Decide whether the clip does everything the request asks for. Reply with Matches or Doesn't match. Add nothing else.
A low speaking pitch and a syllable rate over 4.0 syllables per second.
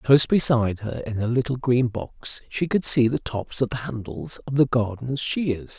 Matches